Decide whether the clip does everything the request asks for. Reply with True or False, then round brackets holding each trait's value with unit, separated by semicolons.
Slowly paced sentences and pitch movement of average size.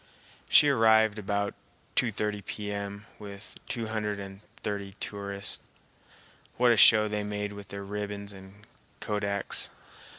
False (125 wpm; 1.1 semitones)